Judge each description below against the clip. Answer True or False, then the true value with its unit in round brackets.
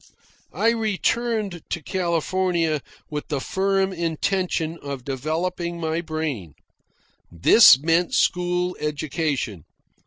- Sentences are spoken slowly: True (95 wpm)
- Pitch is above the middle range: False (170 Hz)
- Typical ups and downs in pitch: True (3.5 semitones)